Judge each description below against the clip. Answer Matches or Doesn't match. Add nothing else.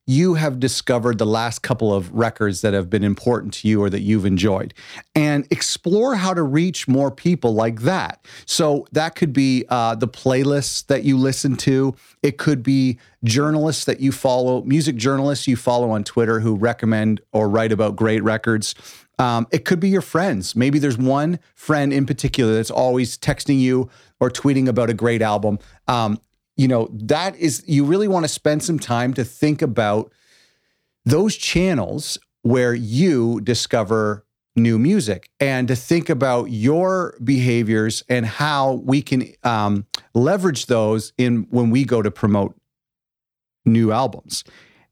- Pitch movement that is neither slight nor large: Matches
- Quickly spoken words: Doesn't match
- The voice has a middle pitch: Doesn't match